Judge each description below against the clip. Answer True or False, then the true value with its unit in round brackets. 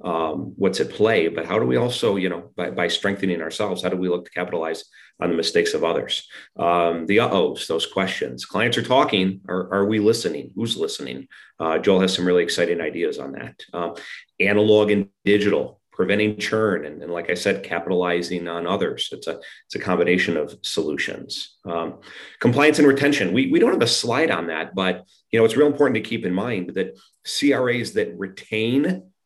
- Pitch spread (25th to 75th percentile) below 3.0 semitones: False (4.3 semitones)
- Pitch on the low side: True (100 Hz)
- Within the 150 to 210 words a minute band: True (200 wpm)